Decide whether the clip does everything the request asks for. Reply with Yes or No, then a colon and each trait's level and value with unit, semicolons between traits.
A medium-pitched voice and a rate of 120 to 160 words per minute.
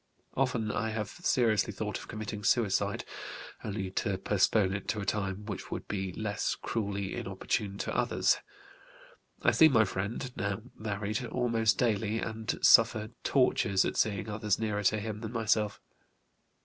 No: low, 105 Hz; average, 150 wpm